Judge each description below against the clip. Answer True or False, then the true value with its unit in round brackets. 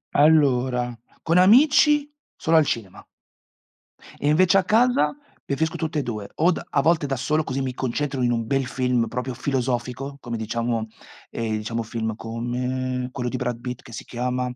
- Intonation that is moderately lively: True (4.1 semitones)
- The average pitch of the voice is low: True (125 Hz)